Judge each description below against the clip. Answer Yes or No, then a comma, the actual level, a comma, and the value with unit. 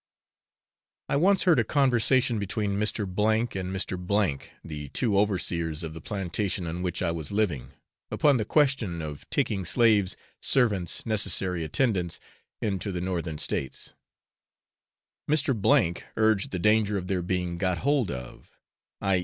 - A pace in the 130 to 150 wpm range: Yes, average, 145 wpm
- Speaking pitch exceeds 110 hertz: No, very low, 95 Hz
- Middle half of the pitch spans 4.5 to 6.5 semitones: No, average, 4.0 semitones